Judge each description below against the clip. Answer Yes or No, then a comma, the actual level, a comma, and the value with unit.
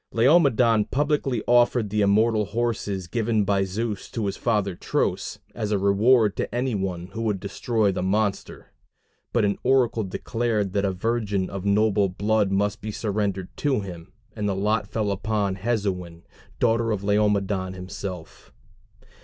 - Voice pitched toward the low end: Yes, low, 105 Hz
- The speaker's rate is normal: Yes, average, 155 wpm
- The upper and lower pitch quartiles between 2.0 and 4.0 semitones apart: Yes, average, 2.7 semitones